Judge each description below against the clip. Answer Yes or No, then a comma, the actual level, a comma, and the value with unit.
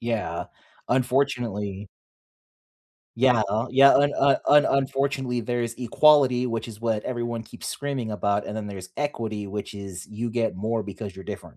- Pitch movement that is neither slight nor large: Yes, average, 3.8 semitones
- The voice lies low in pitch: Yes, low, 115 Hz